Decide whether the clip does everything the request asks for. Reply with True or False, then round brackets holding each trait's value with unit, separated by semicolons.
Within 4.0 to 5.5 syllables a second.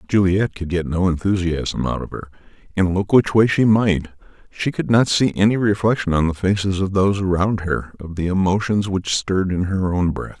True (5.2 syllables/s)